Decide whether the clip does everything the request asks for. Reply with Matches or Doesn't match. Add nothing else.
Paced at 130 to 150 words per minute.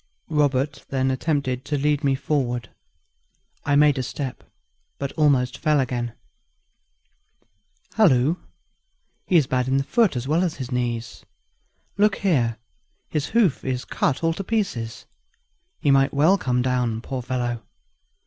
Matches